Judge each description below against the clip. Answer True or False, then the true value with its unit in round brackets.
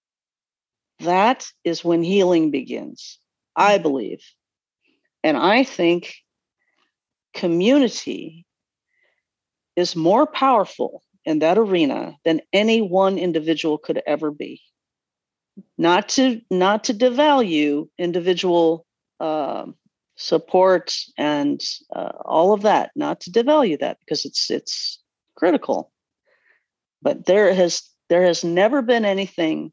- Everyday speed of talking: False (105 wpm)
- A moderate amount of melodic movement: False (7.8 semitones)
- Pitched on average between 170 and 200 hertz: True (190 Hz)